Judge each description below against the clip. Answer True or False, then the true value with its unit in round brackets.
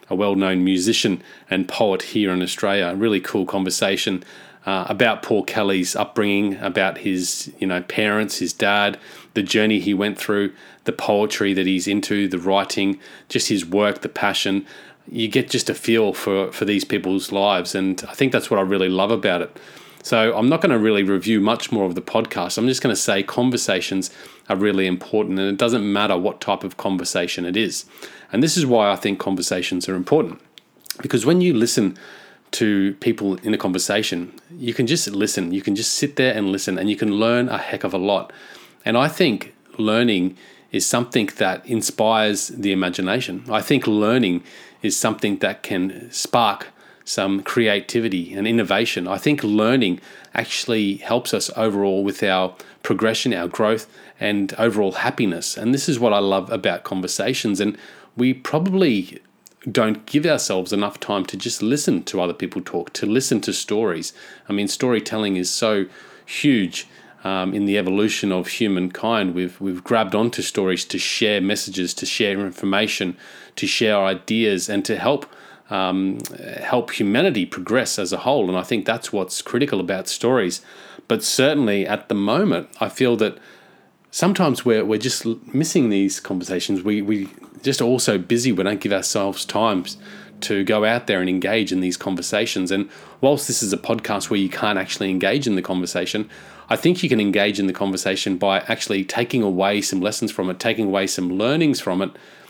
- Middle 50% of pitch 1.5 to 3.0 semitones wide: True (2.7 semitones)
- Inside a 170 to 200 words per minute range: True (180 wpm)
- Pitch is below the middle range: True (100 Hz)